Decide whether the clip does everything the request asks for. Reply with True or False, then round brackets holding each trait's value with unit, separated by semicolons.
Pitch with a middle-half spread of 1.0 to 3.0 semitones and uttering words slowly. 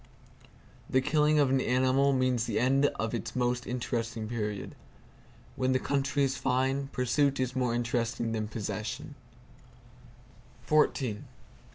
True (2.4 semitones; 125 wpm)